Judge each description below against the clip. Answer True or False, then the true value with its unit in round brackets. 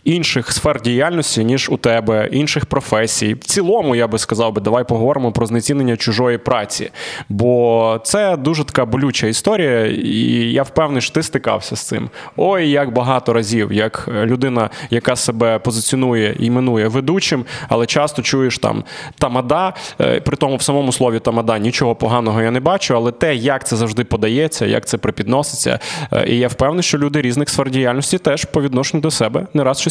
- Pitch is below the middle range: True (125 Hz)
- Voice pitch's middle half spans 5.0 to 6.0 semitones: False (3.7 semitones)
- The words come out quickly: True (170 wpm)